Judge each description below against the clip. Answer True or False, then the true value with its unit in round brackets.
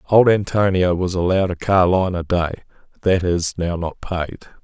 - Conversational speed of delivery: True (170 wpm)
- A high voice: False (90 Hz)